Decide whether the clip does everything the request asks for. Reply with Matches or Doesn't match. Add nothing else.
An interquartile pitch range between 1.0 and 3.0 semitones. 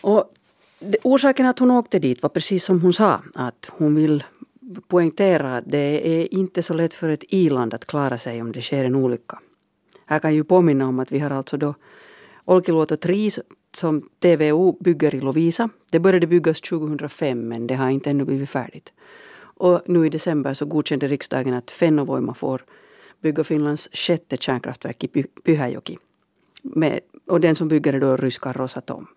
Doesn't match